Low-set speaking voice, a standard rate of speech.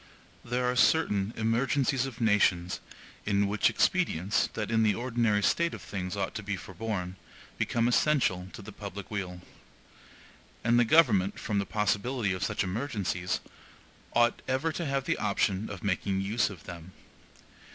Yes: low, 105 Hz; average, 155 wpm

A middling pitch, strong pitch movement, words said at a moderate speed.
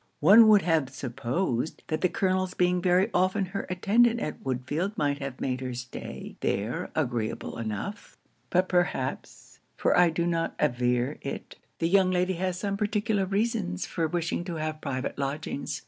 Yes: medium, 170 Hz; wide, 5.9 semitones; average, 165 wpm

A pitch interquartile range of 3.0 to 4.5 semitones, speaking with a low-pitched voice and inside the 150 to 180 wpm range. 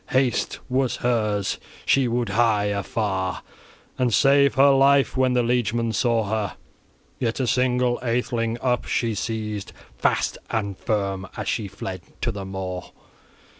No: average, 3.5 semitones; low, 115 Hz; average, 140 wpm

